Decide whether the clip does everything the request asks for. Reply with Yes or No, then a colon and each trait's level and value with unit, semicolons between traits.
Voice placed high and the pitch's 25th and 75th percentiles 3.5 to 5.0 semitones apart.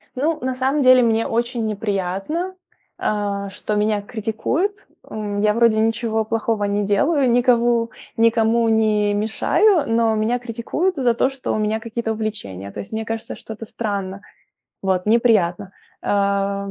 No: high, 220 Hz; narrow, 2.6 semitones